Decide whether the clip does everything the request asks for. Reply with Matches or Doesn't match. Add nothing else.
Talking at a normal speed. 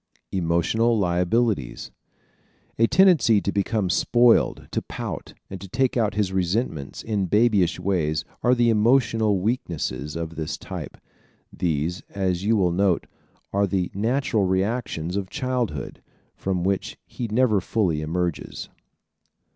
Doesn't match